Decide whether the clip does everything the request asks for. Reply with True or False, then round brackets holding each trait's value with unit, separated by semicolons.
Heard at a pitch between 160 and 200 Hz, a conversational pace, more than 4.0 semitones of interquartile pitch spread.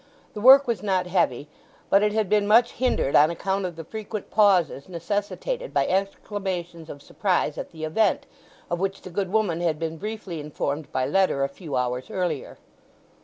True (185 Hz; 180 wpm; 4.5 semitones)